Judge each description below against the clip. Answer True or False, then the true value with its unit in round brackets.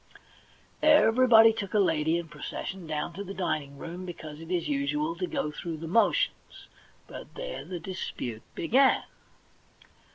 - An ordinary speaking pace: True (150 wpm)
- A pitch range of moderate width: False (6.9 semitones)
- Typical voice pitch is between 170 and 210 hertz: True (185 Hz)